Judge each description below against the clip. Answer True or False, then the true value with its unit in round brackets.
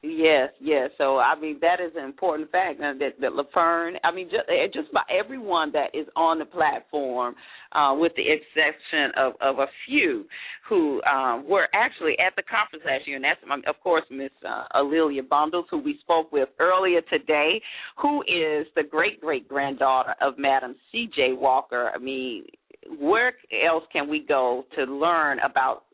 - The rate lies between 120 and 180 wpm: True (175 wpm)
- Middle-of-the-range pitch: True (155 Hz)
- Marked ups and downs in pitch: False (4.7 semitones)